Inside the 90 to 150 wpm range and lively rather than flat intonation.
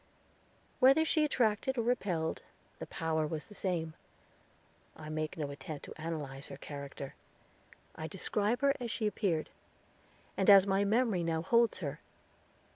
Yes: average, 145 wpm; wide, 6.3 semitones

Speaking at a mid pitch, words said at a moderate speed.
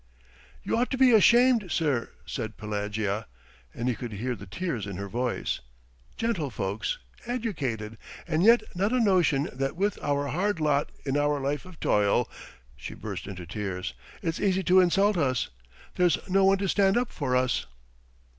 Yes: medium, 145 Hz; average, 165 wpm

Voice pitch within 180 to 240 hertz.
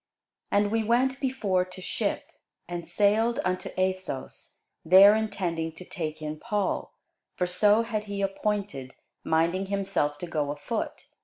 Yes: high, 190 Hz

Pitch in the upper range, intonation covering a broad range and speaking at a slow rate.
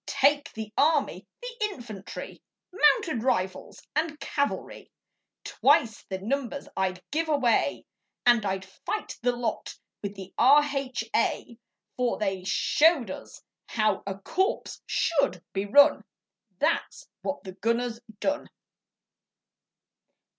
Yes: high, 245 Hz; wide, 6.2 semitones; slow, 110 wpm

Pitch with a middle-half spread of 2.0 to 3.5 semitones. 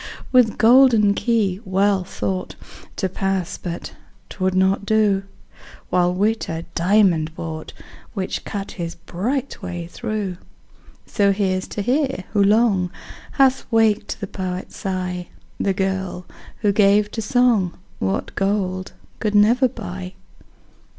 Yes: average, 2.8 semitones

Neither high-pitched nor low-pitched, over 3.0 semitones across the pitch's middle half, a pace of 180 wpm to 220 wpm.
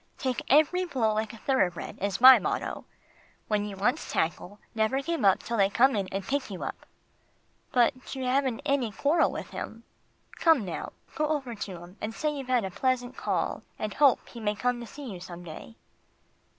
No: high, 240 Hz; average, 4.9 semitones; fast, 205 wpm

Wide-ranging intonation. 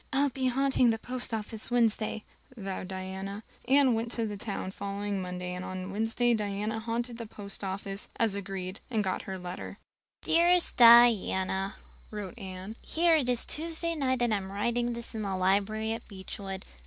No: average, 3.7 semitones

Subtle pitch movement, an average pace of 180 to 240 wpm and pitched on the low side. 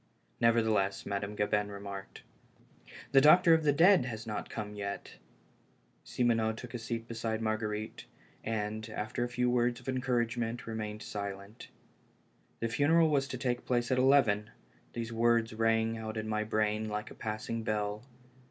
No: narrow, 2.3 semitones; average, 150 wpm; low, 115 Hz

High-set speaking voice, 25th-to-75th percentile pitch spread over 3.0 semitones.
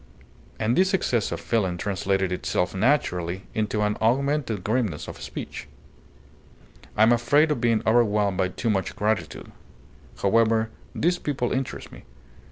No: low, 110 Hz; average, 3.9 semitones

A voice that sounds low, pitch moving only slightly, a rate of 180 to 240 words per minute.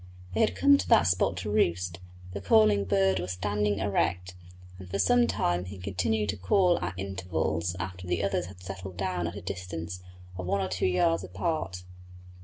Yes: very low, 95 Hz; narrow, 1.7 semitones; average, 190 wpm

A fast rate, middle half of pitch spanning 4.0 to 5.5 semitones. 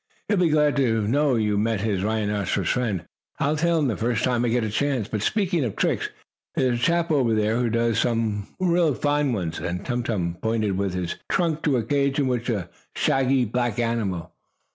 Yes: fast, 210 wpm; average, 4.6 semitones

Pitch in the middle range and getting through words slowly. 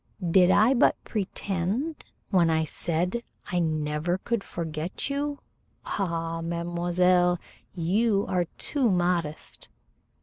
Yes: medium, 180 Hz; slow, 105 wpm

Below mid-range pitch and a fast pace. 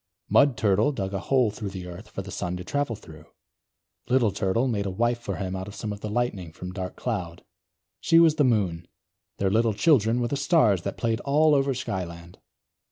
Yes: low, 105 Hz; fast, 210 wpm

